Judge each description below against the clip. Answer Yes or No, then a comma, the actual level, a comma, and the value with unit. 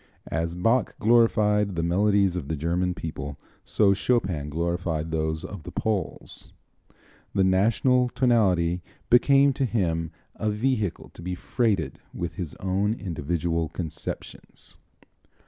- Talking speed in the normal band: No, slow, 125 wpm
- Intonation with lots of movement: No, average, 4.6 semitones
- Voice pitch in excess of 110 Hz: No, very low, 95 Hz